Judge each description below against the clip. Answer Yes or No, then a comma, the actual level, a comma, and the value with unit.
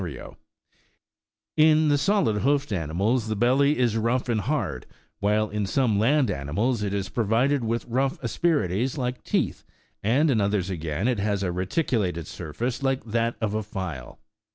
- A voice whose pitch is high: No, low, 115 Hz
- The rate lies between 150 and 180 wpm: Yes, average, 170 wpm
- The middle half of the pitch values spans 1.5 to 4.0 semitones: No, average, 4.8 semitones